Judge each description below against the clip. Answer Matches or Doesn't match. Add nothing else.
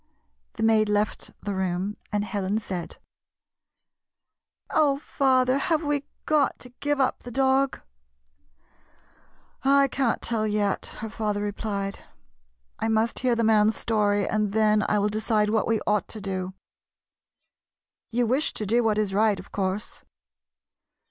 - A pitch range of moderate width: Matches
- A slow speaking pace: Doesn't match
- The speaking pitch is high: Matches